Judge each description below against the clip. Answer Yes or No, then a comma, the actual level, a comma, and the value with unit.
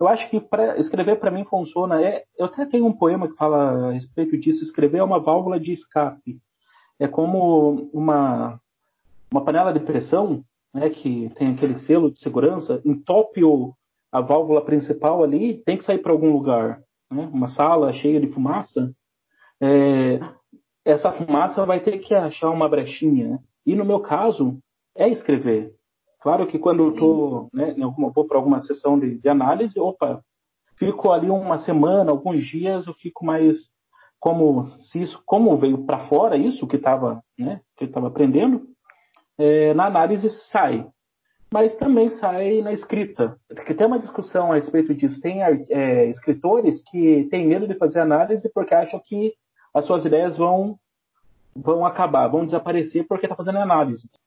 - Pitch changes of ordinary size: Yes, average, 5.0 semitones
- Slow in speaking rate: No, average, 160 wpm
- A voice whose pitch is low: No, medium, 155 Hz